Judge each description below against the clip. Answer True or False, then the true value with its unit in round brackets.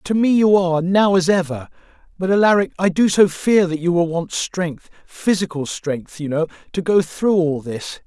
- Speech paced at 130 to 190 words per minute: False (200 wpm)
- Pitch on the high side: False (175 Hz)